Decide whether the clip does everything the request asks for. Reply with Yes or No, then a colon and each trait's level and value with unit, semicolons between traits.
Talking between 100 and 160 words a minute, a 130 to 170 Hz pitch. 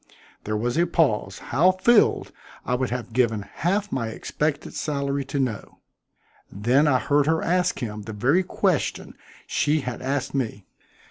Yes: average, 155 wpm; low, 135 Hz